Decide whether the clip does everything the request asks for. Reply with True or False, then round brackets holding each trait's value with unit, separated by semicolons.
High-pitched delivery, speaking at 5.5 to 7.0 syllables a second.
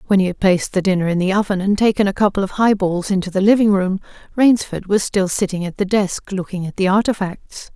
True (195 Hz; 6.0 syllables/s)